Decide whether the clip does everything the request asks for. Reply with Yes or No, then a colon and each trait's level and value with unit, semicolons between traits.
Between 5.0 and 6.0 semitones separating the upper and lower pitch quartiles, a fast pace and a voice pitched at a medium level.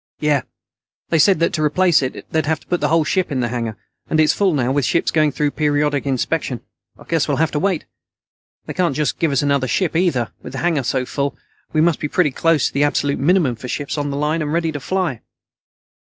No: average, 2.9 semitones; fast, 230 wpm; medium, 150 Hz